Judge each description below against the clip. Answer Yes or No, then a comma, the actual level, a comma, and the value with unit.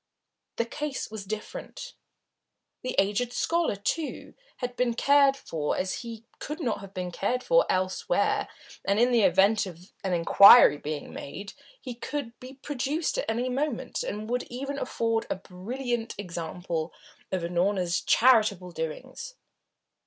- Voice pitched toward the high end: Yes, high, 225 Hz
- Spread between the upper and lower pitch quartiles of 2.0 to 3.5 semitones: No, wide, 5.5 semitones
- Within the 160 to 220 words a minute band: No, average, 145 wpm